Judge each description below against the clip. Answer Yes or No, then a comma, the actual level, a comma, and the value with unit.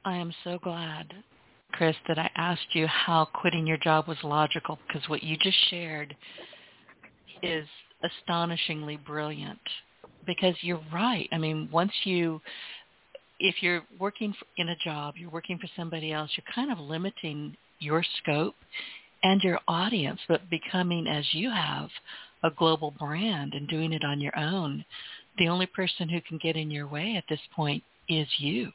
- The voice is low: No, medium, 165 Hz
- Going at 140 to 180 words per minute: Yes, average, 165 wpm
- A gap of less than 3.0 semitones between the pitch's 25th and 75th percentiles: Yes, narrow, 2.6 semitones